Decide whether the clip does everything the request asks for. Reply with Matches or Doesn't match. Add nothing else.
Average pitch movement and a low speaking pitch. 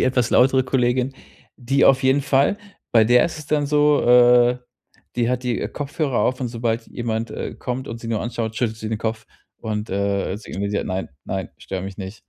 Matches